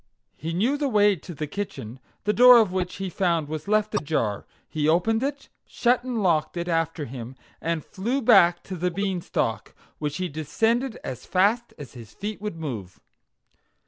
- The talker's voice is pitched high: No, medium, 180 Hz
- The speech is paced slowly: No, average, 175 wpm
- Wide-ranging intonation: Yes, wide, 5.7 semitones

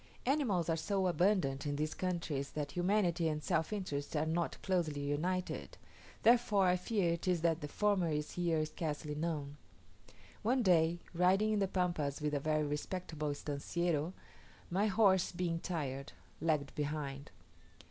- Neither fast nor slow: Yes, average, 150 wpm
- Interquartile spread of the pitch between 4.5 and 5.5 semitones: No, average, 3.6 semitones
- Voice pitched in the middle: Yes, medium, 165 Hz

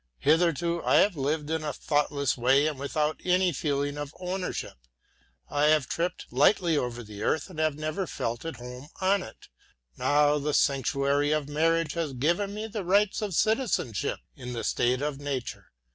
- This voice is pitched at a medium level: Yes, medium, 150 Hz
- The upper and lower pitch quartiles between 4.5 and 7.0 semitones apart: No, average, 3.6 semitones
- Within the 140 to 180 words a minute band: Yes, average, 175 wpm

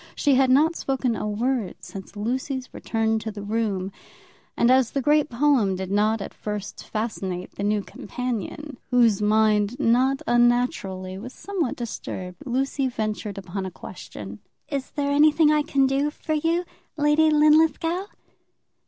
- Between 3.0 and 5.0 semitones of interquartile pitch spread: No, wide, 5.4 semitones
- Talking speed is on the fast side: No, average, 150 wpm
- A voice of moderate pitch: No, high, 240 Hz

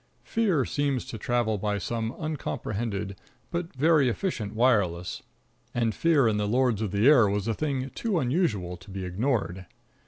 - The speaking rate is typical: Yes, average, 160 wpm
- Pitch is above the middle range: No, low, 115 Hz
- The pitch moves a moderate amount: No, wide, 5.7 semitones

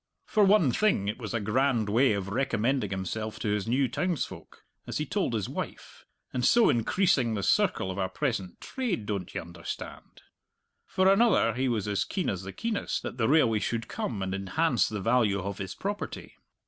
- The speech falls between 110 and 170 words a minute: No, average, 190 wpm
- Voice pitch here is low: Yes, low, 115 Hz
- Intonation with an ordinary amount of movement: No, wide, 5.9 semitones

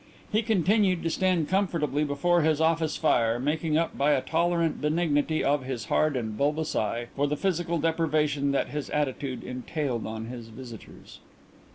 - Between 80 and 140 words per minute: No, average, 165 wpm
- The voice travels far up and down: No, average, 3.9 semitones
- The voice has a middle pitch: Yes, medium, 150 Hz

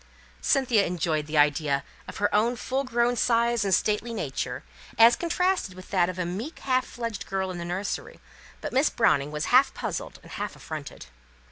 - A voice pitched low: No, high, 205 Hz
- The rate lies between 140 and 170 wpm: No, average, 180 wpm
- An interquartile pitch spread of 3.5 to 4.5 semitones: No, wide, 5.6 semitones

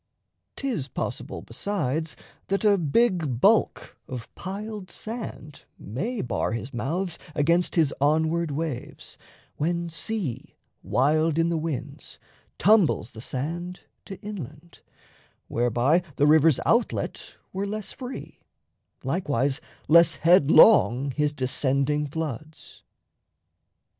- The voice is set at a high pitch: No, medium, 160 Hz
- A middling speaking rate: No, slow, 105 wpm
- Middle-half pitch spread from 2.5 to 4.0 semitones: No, average, 5.1 semitones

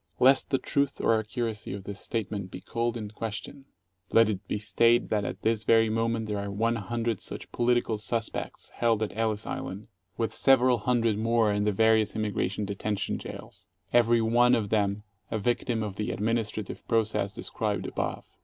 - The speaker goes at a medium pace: Yes, average, 175 wpm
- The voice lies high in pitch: No, low, 110 Hz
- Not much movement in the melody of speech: Yes, narrow, 1.9 semitones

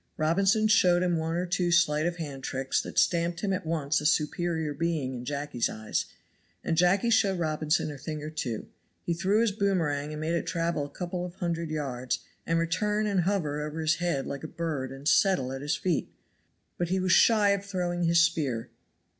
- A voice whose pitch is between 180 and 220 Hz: No, medium, 165 Hz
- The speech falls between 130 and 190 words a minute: No, fast, 205 wpm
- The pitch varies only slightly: No, average, 3.3 semitones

